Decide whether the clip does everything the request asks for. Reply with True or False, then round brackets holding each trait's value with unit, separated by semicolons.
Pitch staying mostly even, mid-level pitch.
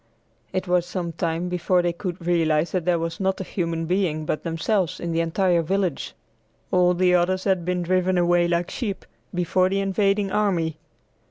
True (1.9 semitones; 180 Hz)